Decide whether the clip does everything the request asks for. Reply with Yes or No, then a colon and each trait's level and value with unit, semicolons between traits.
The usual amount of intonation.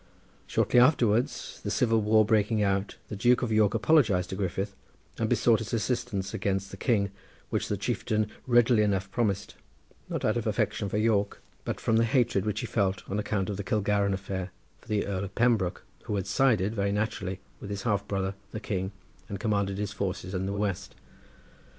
No: narrow, 2.1 semitones